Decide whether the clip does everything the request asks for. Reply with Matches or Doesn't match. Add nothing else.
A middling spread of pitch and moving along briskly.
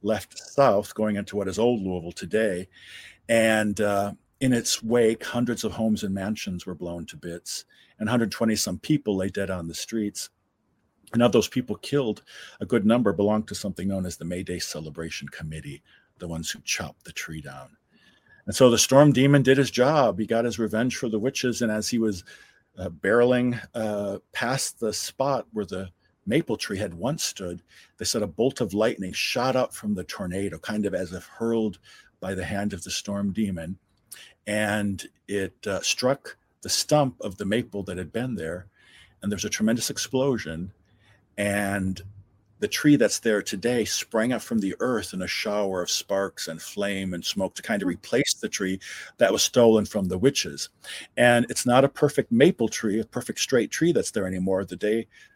Doesn't match